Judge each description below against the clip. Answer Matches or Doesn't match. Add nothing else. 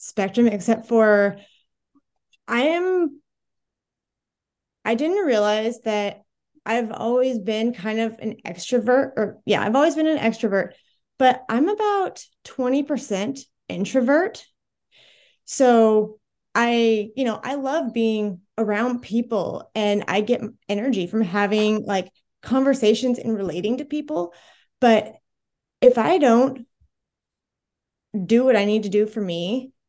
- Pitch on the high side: Matches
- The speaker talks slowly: Matches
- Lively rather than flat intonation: Doesn't match